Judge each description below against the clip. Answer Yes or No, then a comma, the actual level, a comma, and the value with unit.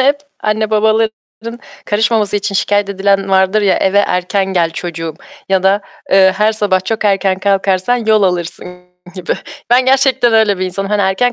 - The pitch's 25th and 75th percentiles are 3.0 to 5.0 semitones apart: No, narrow, 2.4 semitones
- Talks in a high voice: Yes, high, 200 Hz